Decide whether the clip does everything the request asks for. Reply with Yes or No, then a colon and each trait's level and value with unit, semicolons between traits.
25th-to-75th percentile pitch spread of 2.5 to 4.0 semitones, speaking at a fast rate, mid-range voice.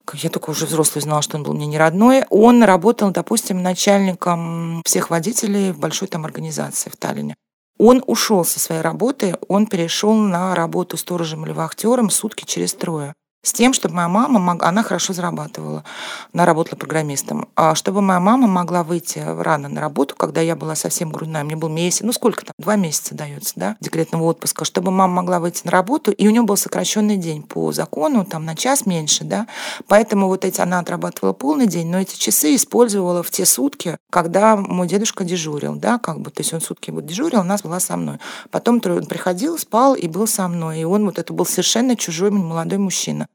No: average, 4.4 semitones; fast, 200 wpm; medium, 180 Hz